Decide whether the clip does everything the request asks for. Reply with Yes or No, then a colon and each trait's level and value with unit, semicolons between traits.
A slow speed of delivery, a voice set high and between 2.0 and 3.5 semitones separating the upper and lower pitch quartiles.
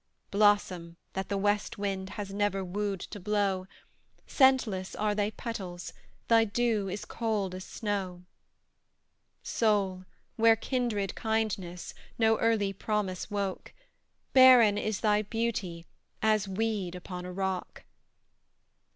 Yes: slow, 115 wpm; high, 205 Hz; narrow, 2.5 semitones